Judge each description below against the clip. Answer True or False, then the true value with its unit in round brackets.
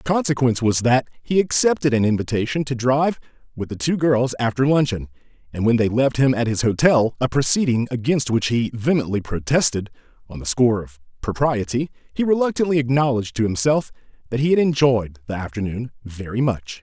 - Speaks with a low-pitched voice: True (125 Hz)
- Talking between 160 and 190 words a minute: True (175 wpm)